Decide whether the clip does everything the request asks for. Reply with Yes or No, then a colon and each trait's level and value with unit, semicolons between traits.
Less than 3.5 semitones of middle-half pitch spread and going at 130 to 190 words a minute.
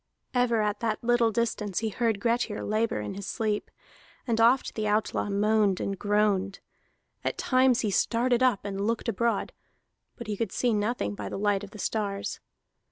Yes: narrow, 2.5 semitones; average, 175 wpm